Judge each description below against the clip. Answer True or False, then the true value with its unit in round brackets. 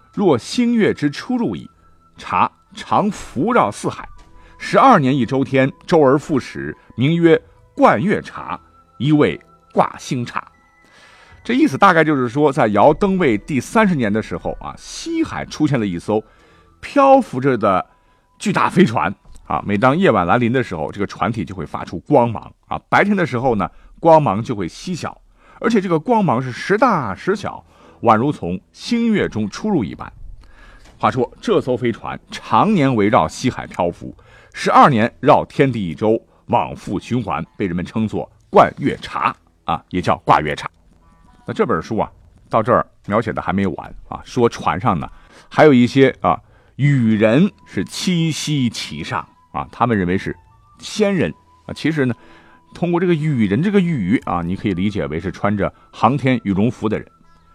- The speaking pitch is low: True (130 Hz)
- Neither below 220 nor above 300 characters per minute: True (240 characters per minute)